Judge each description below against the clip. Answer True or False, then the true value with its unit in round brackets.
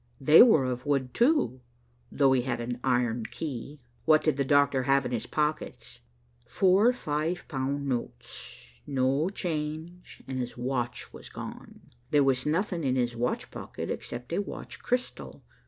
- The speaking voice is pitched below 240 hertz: True (140 Hz)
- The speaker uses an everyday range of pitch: True (3.8 semitones)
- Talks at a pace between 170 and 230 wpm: False (155 wpm)